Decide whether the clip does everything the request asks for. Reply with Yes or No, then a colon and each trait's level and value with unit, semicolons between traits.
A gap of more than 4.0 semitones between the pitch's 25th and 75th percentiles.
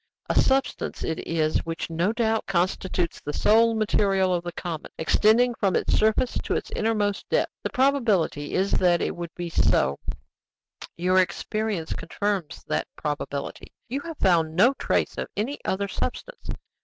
Yes: average, 4.6 semitones